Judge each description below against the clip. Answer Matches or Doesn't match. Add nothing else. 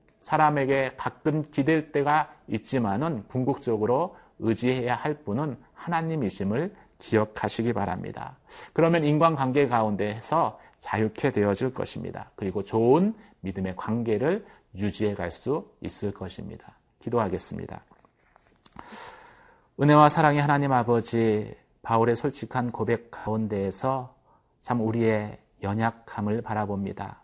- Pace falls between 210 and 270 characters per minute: Doesn't match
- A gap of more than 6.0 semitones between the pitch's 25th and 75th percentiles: Doesn't match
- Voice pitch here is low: Matches